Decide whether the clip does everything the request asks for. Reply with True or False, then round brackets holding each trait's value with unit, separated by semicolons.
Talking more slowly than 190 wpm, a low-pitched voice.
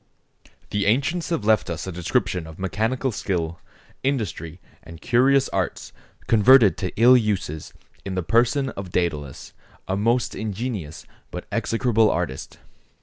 True (135 wpm; 105 Hz)